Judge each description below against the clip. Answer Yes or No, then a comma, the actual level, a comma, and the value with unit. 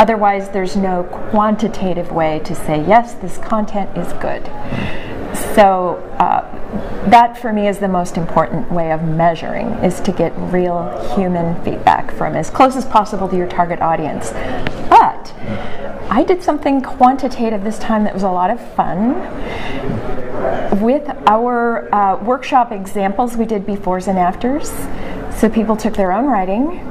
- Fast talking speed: No, average, 150 wpm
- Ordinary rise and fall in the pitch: Yes, average, 4.3 semitones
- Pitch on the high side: Yes, high, 205 Hz